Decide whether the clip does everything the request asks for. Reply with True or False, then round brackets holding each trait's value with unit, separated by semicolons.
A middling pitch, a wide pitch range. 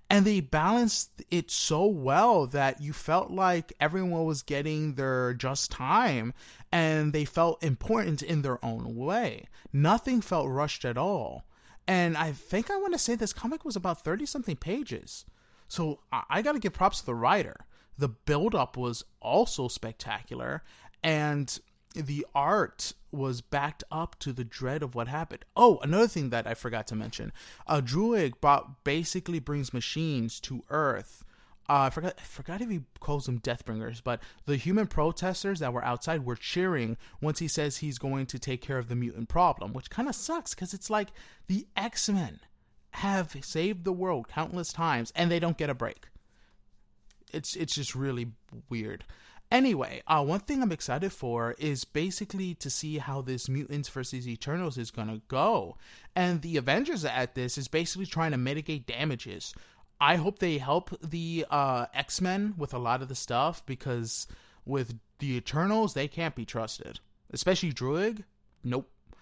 True (150 Hz; 6.0 semitones)